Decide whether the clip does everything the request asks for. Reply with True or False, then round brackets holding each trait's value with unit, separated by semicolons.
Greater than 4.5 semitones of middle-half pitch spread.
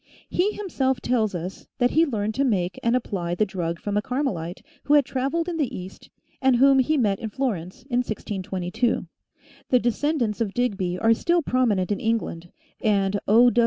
True (5.4 semitones)